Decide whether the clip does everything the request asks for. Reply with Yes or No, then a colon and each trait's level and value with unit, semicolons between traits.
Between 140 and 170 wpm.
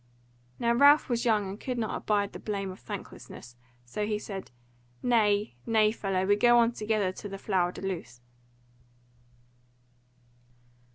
Yes: average, 150 wpm